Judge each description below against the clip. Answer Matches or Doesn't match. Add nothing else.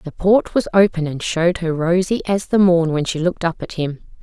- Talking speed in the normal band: Doesn't match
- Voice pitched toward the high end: Doesn't match